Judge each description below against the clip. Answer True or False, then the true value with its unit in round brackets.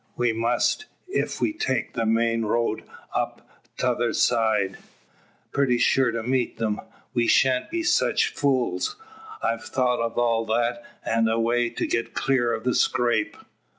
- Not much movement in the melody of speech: True (1.7 semitones)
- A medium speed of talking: True (150 wpm)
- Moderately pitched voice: False (120 Hz)